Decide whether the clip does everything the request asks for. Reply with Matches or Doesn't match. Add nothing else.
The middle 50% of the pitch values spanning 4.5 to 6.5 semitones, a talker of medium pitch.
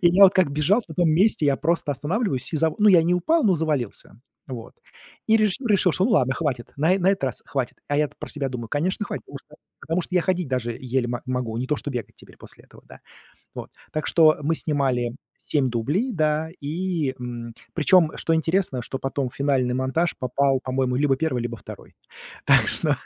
Matches